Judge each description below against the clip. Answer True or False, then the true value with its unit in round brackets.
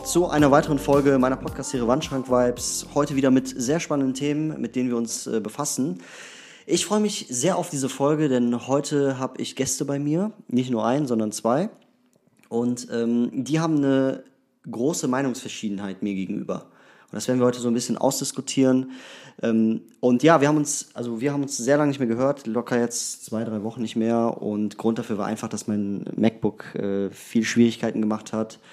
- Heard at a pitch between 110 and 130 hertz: True (125 Hz)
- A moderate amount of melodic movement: True (3.8 semitones)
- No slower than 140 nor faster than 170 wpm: False (190 wpm)